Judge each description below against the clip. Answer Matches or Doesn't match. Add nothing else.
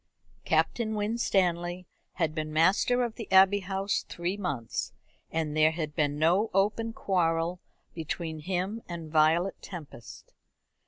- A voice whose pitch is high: Doesn't match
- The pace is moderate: Doesn't match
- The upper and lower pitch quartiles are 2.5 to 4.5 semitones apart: Matches